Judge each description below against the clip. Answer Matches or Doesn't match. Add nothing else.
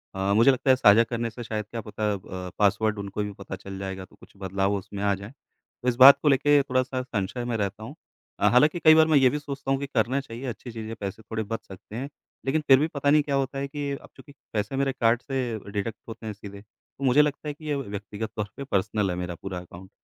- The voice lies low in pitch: Matches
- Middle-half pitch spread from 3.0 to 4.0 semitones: Doesn't match